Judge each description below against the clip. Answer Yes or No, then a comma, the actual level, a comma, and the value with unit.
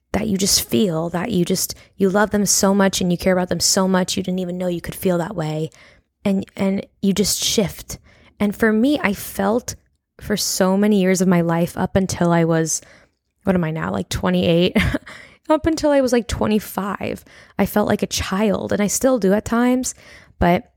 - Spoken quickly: Yes, fast, 210 wpm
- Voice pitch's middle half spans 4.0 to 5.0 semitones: No, average, 2.8 semitones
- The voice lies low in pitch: No, high, 195 Hz